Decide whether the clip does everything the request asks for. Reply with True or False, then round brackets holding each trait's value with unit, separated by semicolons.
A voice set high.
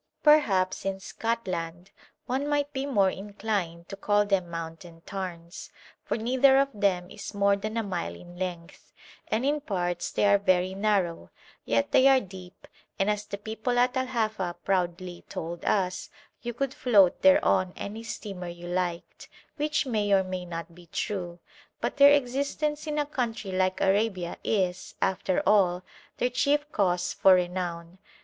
True (195 Hz)